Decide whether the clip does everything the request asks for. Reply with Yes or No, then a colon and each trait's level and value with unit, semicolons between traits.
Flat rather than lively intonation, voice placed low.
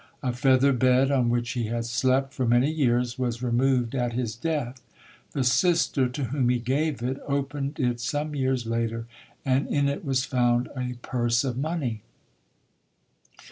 Yes: narrow, 2.3 semitones; low, 130 Hz